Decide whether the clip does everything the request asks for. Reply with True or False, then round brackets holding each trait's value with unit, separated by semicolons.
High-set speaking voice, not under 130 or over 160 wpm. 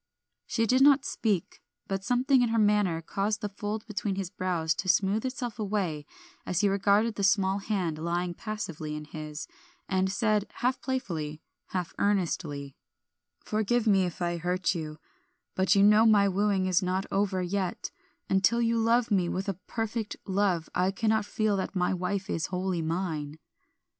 False (195 Hz; 170 wpm)